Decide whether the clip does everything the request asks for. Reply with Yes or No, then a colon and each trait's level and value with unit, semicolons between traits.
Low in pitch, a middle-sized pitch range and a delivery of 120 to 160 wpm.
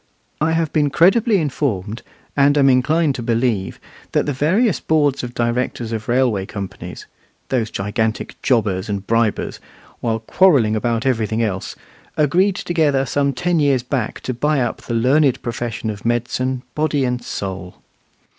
Yes: low, 125 Hz; average, 4.5 semitones; average, 150 wpm